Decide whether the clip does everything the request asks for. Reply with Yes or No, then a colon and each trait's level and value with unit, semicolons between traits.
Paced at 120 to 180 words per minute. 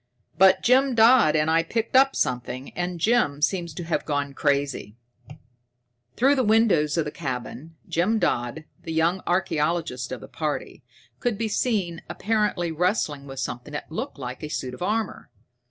Yes: average, 165 wpm